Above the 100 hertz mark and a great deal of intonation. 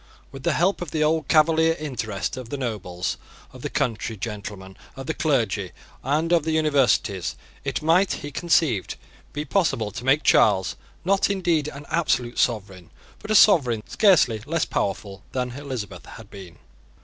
Yes: low, 135 Hz; wide, 7.0 semitones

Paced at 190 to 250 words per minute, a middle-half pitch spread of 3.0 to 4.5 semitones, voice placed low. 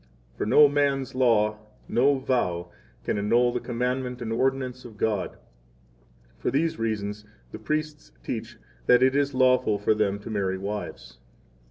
No: average, 155 wpm; average, 3.9 semitones; low, 120 Hz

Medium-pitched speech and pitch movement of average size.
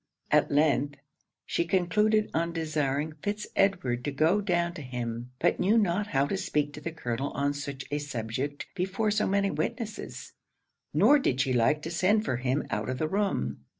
No: medium, 155 Hz; wide, 6.3 semitones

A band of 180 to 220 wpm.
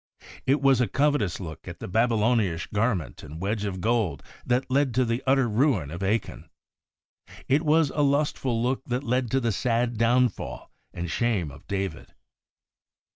No: average, 165 wpm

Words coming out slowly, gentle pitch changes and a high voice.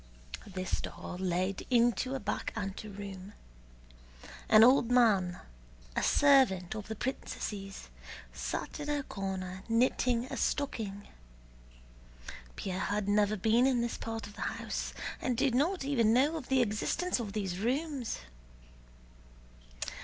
No: slow, 130 wpm; average, 4.7 semitones; high, 220 Hz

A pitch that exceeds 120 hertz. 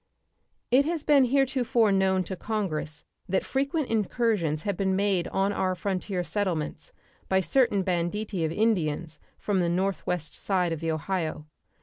Yes: high, 190 Hz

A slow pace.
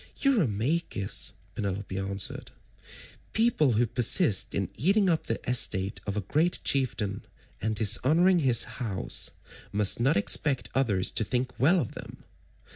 Yes: slow, 130 wpm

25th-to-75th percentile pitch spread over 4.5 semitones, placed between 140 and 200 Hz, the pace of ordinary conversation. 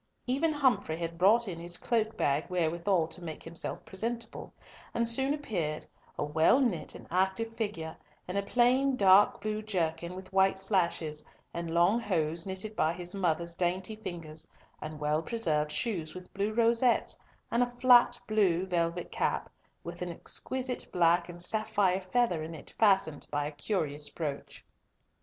Yes: average, 5.0 semitones; medium, 185 Hz; average, 160 wpm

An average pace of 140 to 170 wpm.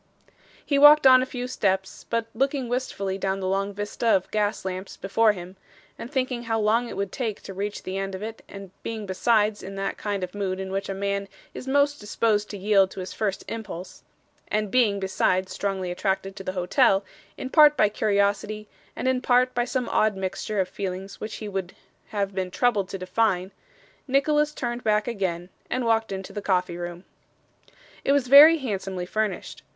No: average, 195 wpm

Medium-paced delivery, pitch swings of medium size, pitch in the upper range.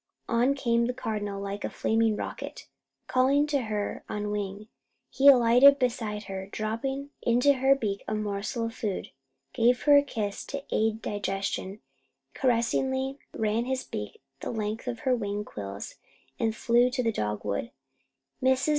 Yes: average, 155 wpm; average, 3.7 semitones; high, 225 Hz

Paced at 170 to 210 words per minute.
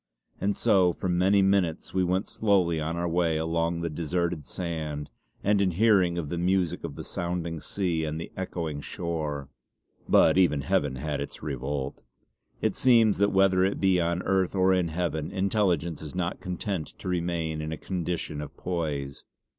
Yes: average, 175 wpm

